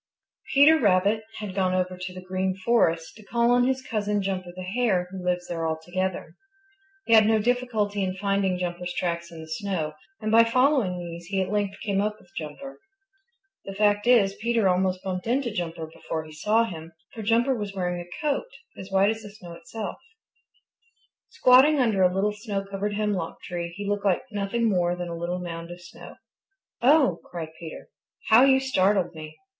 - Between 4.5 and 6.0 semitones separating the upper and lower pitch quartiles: No, average, 3.7 semitones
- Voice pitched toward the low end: No, high, 195 Hz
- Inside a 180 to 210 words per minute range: Yes, average, 190 wpm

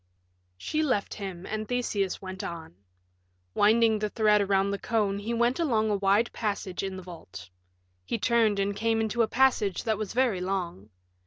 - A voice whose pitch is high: Yes, high, 205 Hz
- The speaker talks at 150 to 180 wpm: Yes, average, 175 wpm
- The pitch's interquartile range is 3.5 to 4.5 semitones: No, average, 2.9 semitones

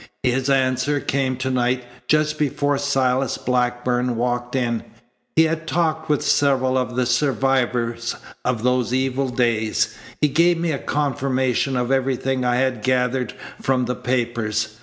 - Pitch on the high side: No, low, 130 Hz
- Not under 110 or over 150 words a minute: Yes, average, 145 wpm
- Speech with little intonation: Yes, narrow, 2.0 semitones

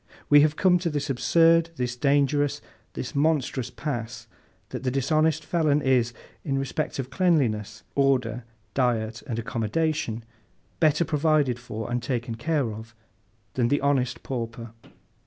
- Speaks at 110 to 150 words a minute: Yes, average, 140 wpm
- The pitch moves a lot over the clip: No, average, 4.3 semitones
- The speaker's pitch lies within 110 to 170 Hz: Yes, low, 135 Hz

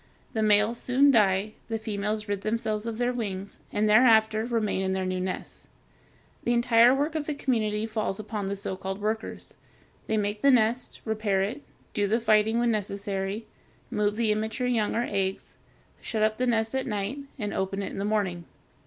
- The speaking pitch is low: No, high, 215 Hz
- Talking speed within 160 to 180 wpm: No, average, 190 wpm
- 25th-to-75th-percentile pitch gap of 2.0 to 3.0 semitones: Yes, narrow, 2.4 semitones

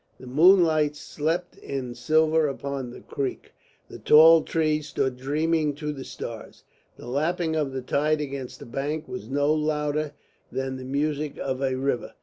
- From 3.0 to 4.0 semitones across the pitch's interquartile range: No, narrow, 2.6 semitones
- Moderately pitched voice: Yes, medium, 150 Hz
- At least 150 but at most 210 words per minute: Yes, average, 160 wpm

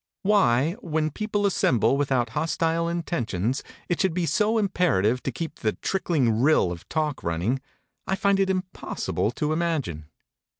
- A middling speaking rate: Yes, average, 145 wpm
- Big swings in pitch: Yes, wide, 7.0 semitones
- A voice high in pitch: No, medium, 155 Hz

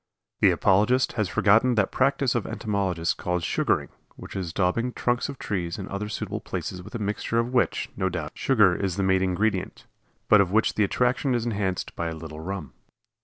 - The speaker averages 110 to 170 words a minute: No, average, 195 wpm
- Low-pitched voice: Yes, low, 100 Hz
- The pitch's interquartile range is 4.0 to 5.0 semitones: Yes, average, 4.3 semitones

